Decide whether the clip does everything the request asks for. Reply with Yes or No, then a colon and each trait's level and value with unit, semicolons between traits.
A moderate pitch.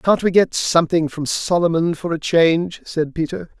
Yes: medium, 165 Hz